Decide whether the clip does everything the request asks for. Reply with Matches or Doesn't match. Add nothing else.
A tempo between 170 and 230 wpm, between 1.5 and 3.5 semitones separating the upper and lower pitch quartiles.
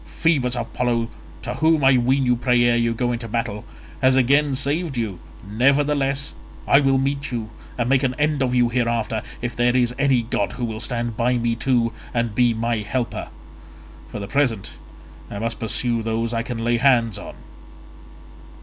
Matches